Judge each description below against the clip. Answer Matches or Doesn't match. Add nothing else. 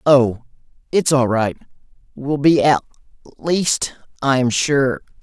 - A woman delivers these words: Doesn't match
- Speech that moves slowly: Matches